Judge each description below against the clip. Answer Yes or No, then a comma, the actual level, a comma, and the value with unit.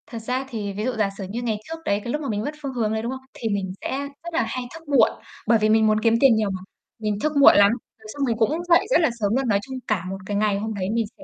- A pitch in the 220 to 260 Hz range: Yes, high, 225 Hz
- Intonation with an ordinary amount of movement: Yes, average, 4.3 semitones